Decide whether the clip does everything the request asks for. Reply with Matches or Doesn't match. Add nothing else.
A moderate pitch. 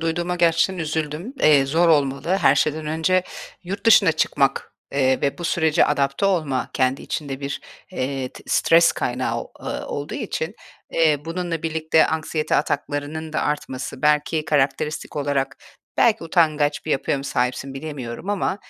Matches